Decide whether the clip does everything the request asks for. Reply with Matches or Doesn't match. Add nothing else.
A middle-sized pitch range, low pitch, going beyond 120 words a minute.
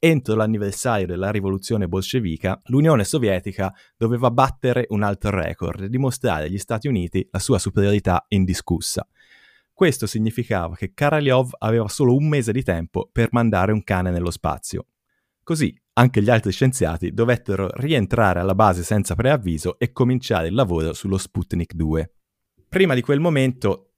Matches